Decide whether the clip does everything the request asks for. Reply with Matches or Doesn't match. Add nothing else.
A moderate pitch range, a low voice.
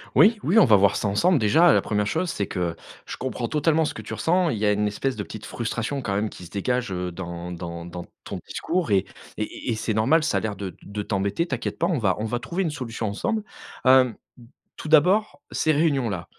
Doesn't match